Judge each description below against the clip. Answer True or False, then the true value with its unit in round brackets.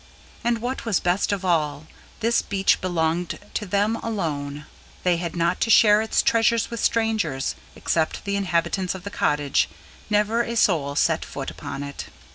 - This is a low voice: False (190 Hz)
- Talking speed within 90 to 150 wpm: False (165 wpm)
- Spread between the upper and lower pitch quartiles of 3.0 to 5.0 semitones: False (5.4 semitones)